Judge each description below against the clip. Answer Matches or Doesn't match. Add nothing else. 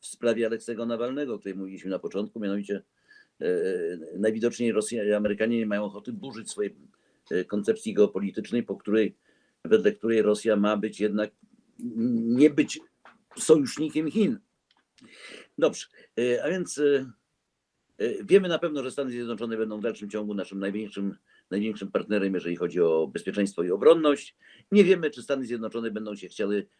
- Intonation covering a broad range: Matches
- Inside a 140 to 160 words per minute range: Matches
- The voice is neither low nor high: Doesn't match